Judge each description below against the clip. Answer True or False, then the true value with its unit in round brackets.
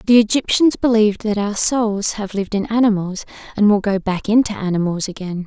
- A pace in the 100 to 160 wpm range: False (185 wpm)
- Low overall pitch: False (210 Hz)